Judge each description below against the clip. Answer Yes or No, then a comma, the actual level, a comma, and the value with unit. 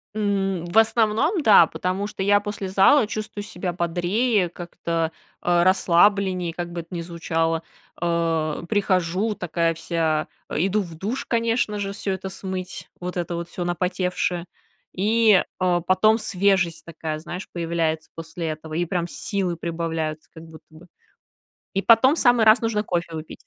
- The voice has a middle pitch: Yes, medium, 180 Hz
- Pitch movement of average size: Yes, average, 3.4 semitones